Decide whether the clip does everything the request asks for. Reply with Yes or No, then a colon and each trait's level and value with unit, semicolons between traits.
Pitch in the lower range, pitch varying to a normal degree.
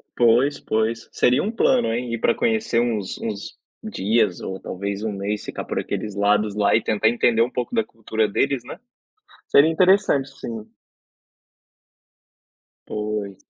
Yes: low, 115 Hz; average, 3.7 semitones